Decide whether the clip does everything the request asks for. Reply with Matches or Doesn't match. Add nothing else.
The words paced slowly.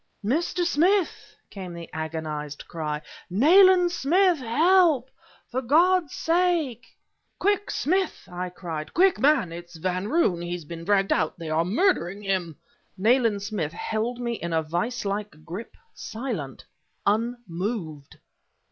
Matches